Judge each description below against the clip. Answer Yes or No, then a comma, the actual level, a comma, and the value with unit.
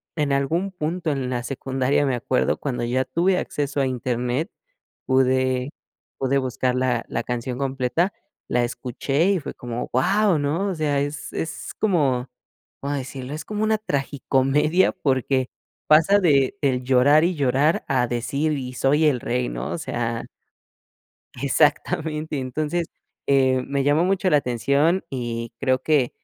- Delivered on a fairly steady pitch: No, average, 3.4 semitones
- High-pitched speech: No, medium, 140 Hz